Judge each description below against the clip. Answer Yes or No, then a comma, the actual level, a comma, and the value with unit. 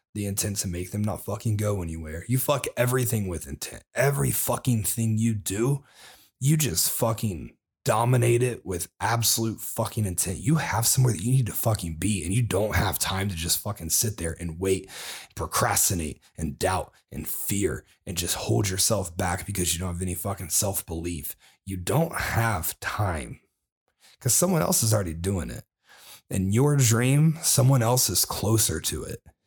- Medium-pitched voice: No, low, 105 Hz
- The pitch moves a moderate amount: Yes, average, 4.7 semitones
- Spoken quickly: No, average, 175 wpm